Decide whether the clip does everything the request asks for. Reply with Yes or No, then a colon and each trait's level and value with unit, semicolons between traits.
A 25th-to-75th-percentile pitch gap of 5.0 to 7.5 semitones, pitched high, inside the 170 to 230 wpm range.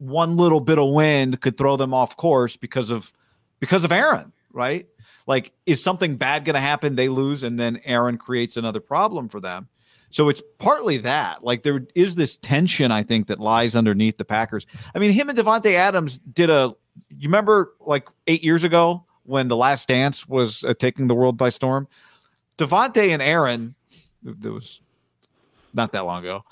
No: average, 5.3 semitones; low, 135 Hz; average, 185 wpm